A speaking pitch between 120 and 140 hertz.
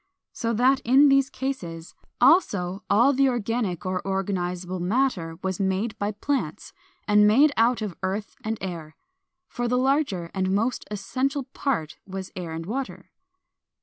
No: high, 210 Hz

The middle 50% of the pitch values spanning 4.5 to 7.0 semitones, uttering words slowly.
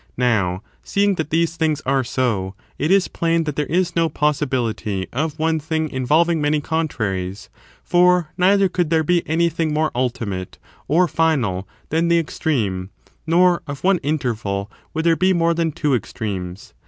No: wide, 5.6 semitones; average, 160 wpm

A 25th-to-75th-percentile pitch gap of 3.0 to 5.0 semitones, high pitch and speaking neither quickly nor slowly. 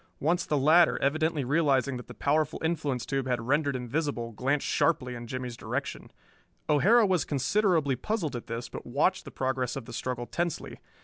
No: average, 4.2 semitones; medium, 140 Hz; average, 180 wpm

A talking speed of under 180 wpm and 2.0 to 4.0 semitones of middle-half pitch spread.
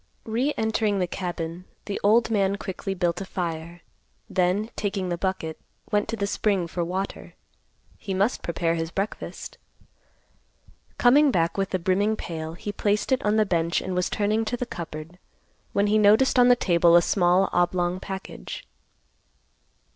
Yes: average, 160 wpm; average, 3.3 semitones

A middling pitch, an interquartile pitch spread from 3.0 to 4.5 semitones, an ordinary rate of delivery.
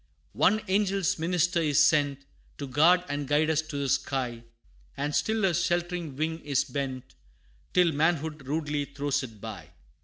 Yes: medium, 150 Hz; average, 3.7 semitones; average, 155 wpm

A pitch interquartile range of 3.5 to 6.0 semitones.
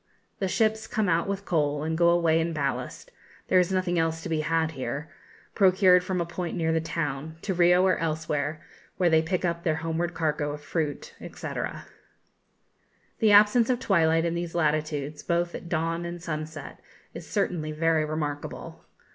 No: narrow, 2.4 semitones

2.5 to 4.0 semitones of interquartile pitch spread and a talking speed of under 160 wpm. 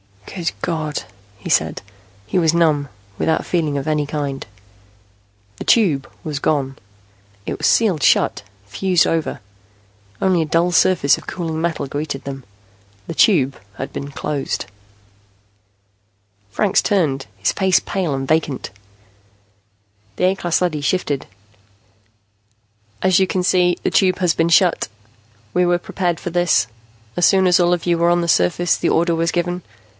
Yes: average, 3.5 semitones; average, 150 wpm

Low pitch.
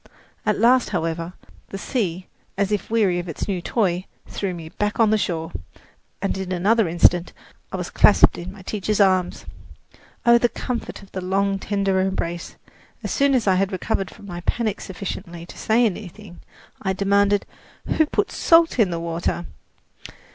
No: high, 195 Hz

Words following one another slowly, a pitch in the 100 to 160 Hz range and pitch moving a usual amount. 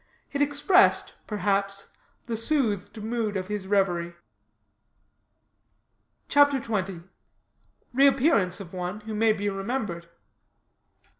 No: slow, 95 wpm; high, 210 Hz; average, 4.0 semitones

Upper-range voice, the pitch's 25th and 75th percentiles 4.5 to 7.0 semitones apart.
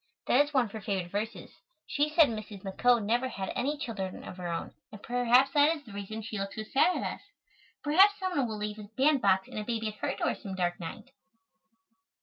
Yes: high, 220 Hz; average, 5.3 semitones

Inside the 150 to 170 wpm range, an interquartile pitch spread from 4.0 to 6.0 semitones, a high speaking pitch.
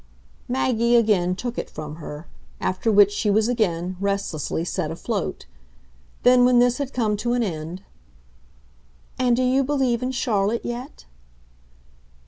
No: average, 140 wpm; average, 4.7 semitones; high, 225 Hz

